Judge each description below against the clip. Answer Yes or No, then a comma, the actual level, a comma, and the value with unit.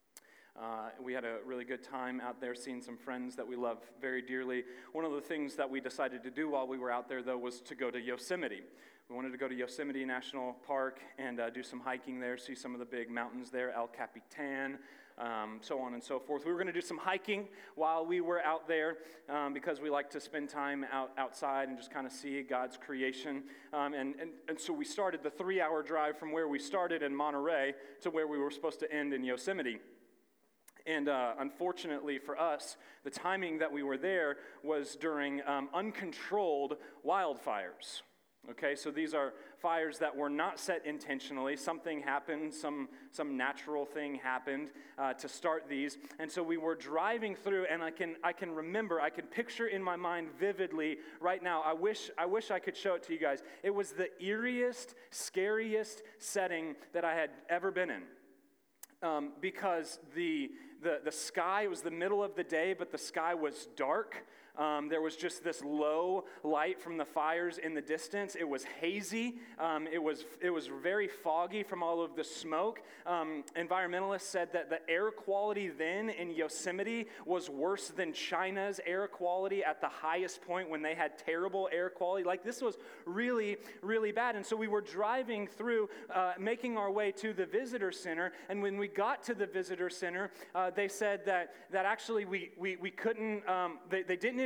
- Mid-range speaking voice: Yes, medium, 160 Hz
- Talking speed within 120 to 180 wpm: No, average, 200 wpm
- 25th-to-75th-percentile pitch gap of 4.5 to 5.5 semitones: Yes, average, 5.1 semitones